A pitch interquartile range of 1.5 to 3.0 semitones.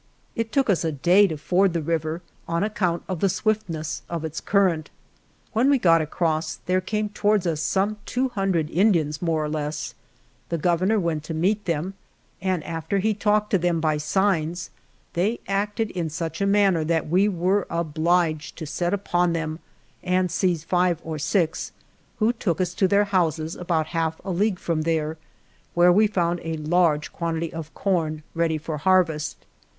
No: average, 3.4 semitones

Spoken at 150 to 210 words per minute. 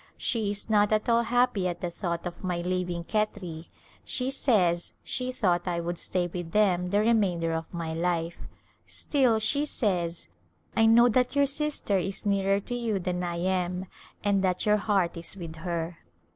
Yes: average, 185 wpm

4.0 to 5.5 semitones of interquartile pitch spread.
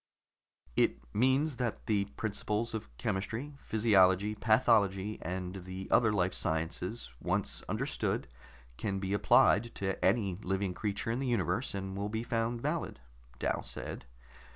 No: average, 3.2 semitones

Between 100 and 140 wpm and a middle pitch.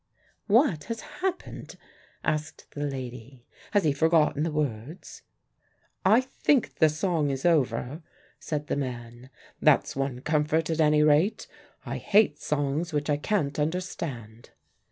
Yes: slow, 135 wpm; medium, 150 Hz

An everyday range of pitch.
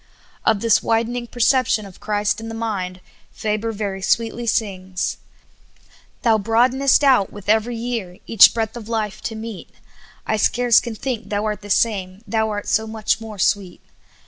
No: narrow, 2.0 semitones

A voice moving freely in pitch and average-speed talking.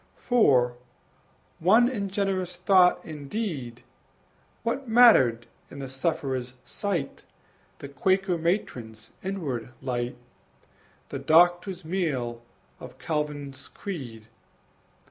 No: wide, 7.0 semitones; slow, 95 wpm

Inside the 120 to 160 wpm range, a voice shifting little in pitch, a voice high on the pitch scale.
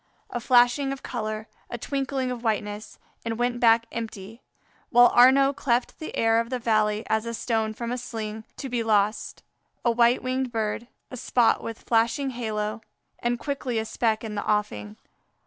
No: average, 175 wpm; narrow, 2.2 semitones; high, 230 Hz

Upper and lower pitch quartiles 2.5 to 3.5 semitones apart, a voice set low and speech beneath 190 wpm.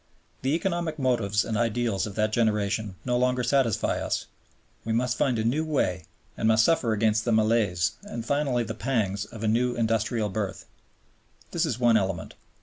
Yes: average, 2.8 semitones; low, 115 Hz; average, 175 wpm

